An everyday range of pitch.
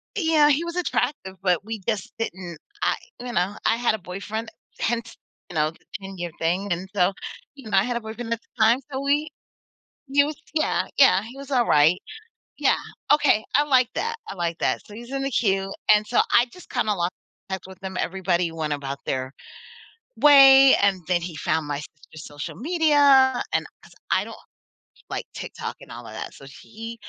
No: wide, 7.0 semitones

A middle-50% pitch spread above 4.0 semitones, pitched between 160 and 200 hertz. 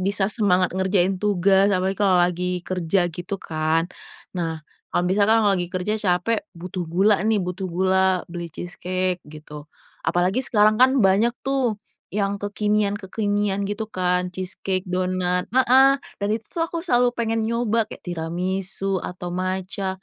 No: narrow, 2.5 semitones; high, 190 Hz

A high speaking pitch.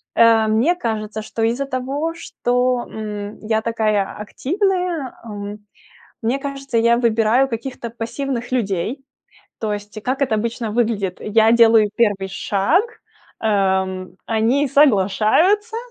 Yes: high, 230 Hz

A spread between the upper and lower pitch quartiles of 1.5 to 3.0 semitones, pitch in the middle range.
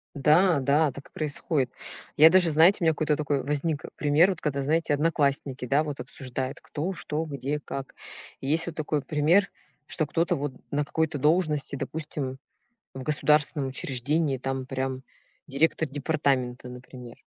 Yes: average, 2.7 semitones; medium, 145 Hz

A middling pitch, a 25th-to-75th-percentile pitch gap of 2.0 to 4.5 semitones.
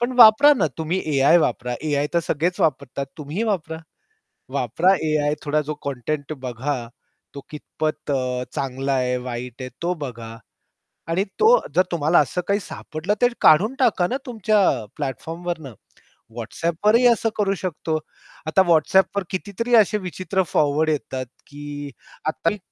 No: medium, 155 Hz; average, 5.2 semitones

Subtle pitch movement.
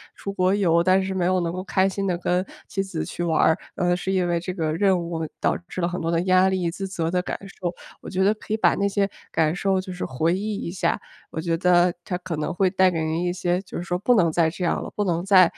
Yes: narrow, 2.0 semitones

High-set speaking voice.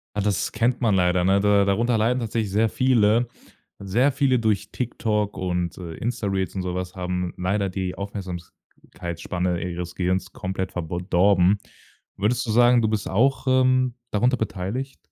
No: low, 100 Hz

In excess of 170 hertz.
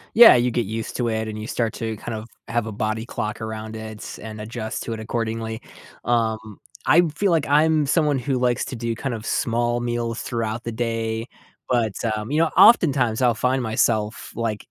No: low, 115 Hz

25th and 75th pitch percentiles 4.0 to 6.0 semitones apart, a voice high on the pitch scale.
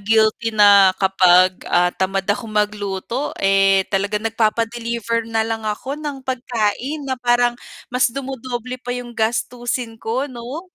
No: average, 3.4 semitones; high, 225 Hz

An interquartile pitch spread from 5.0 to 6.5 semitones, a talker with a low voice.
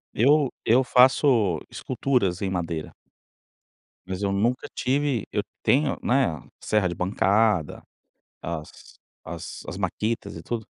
Yes: wide, 5.5 semitones; low, 105 Hz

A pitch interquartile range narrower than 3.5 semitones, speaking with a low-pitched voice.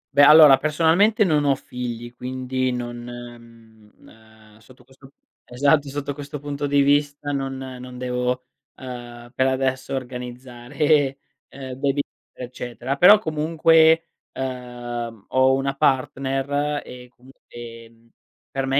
Yes: average, 2.7 semitones; low, 130 Hz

